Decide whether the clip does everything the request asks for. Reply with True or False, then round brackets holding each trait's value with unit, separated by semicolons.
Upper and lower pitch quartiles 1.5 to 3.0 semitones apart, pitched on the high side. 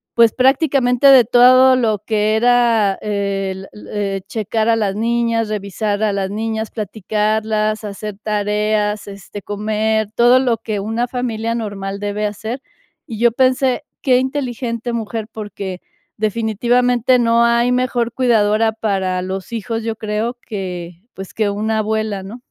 True (2.4 semitones; 220 Hz)